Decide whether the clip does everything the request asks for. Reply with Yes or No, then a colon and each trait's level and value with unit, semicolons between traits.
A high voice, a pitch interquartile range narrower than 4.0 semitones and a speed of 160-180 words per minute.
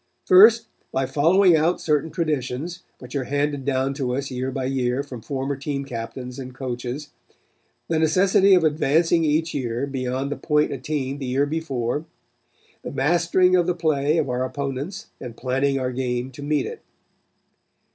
No: medium, 140 Hz; average, 3.6 semitones; average, 165 wpm